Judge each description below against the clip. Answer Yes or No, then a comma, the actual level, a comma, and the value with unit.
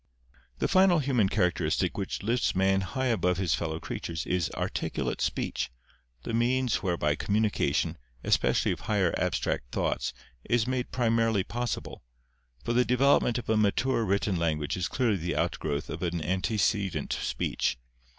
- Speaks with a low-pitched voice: Yes, low, 100 Hz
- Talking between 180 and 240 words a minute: No, average, 145 wpm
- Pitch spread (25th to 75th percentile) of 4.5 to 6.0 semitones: Yes, average, 5.3 semitones